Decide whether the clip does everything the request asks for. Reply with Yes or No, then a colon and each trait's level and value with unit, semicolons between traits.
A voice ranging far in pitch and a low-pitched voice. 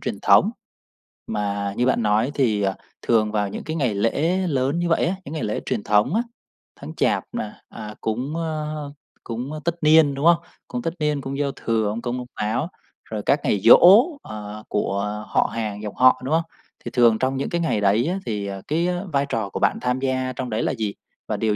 Yes: wide, 6.1 semitones; low, 125 Hz